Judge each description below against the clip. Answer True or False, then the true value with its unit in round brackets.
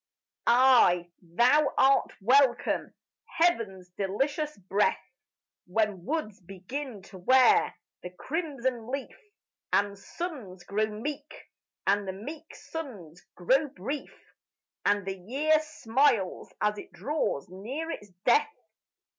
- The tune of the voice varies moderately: False (7.0 semitones)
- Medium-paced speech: False (110 wpm)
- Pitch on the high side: True (230 Hz)